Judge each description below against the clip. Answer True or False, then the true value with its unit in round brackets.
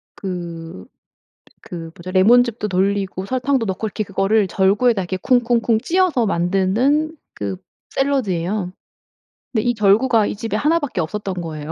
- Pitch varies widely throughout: False (4.8 semitones)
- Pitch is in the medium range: False (205 Hz)